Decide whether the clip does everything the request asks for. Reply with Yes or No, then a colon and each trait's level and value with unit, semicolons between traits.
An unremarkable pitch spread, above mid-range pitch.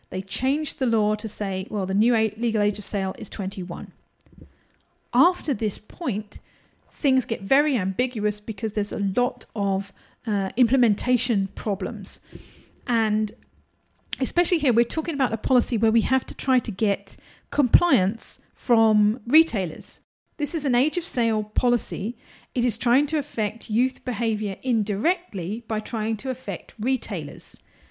Yes: average, 3.7 semitones; high, 230 Hz